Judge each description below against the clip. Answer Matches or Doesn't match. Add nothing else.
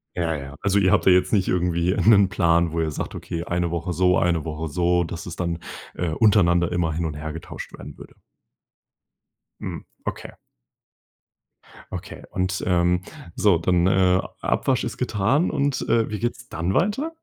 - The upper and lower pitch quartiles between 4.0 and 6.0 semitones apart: Doesn't match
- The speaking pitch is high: Doesn't match